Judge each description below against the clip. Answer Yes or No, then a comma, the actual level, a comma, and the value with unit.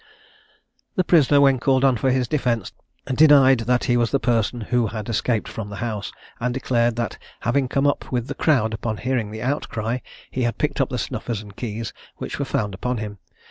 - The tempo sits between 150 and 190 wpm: No, fast, 205 wpm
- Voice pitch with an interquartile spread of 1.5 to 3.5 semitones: Yes, average, 3.0 semitones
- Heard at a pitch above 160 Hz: No, low, 120 Hz